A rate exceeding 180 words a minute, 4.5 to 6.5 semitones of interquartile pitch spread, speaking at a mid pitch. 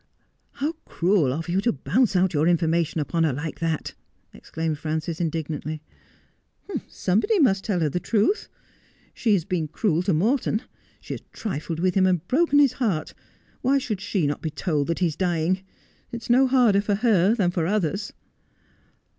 Yes: average, 190 wpm; average, 5.0 semitones; medium, 180 Hz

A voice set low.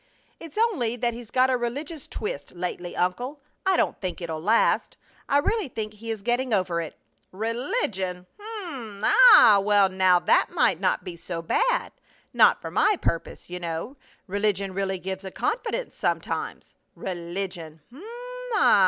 No: high, 210 Hz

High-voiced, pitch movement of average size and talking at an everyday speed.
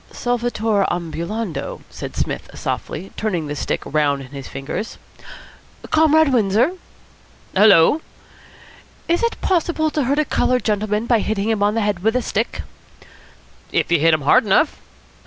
No: high, 215 Hz; wide, 6.4 semitones; average, 150 wpm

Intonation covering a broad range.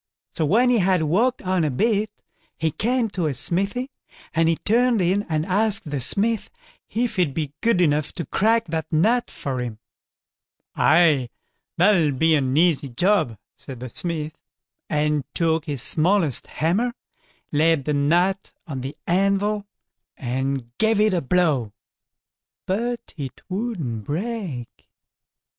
Yes: wide, 6.0 semitones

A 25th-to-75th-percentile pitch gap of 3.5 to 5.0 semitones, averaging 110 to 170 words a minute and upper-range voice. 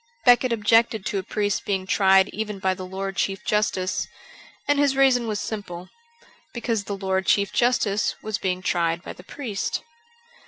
No: average, 3.0 semitones; average, 165 wpm; high, 200 Hz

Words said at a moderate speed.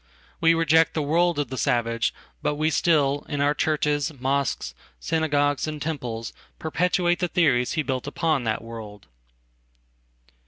No: slow, 130 wpm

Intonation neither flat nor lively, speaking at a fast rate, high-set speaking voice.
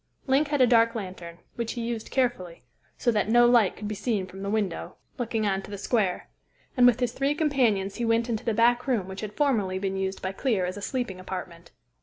Yes: average, 4.1 semitones; fast, 230 wpm; high, 220 Hz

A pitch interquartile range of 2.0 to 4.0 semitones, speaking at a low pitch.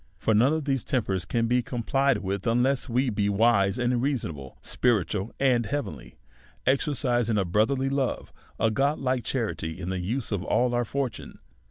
No: average, 4.6 semitones; low, 120 Hz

